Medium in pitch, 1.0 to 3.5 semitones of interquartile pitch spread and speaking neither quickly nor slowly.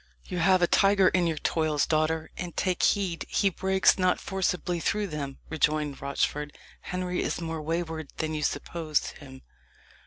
Yes: medium, 165 Hz; average, 3.0 semitones; average, 160 wpm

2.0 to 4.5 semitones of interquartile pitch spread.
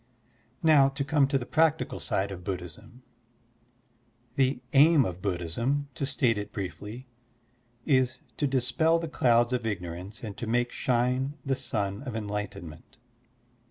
No: average, 5.2 semitones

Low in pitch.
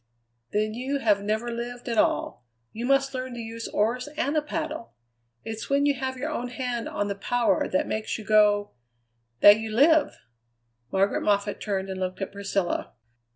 No: high, 230 Hz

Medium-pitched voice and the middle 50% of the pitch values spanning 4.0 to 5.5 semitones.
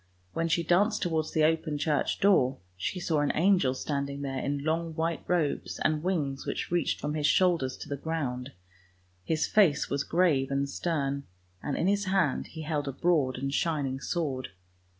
No: medium, 155 Hz; average, 3.4 semitones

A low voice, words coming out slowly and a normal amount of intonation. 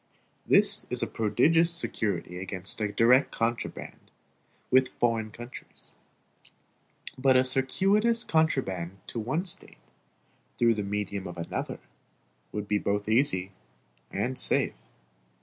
Yes: low, 115 Hz; slow, 115 wpm; average, 4.7 semitones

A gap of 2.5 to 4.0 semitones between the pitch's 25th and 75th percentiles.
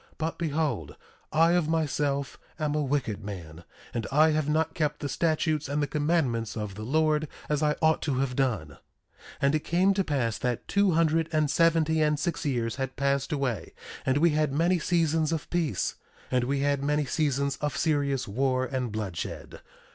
Yes: average, 3.4 semitones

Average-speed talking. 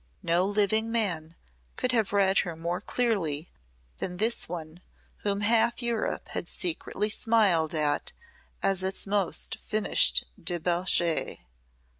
No: slow, 120 wpm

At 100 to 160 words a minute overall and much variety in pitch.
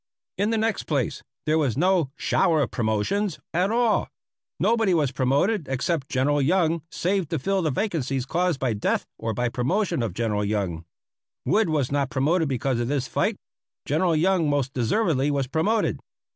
No: average, 170 wpm; wide, 6.1 semitones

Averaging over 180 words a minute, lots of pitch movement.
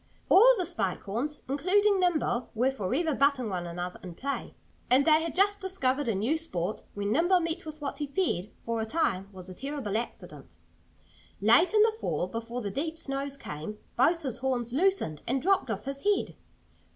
Yes: average, 190 wpm; wide, 7.4 semitones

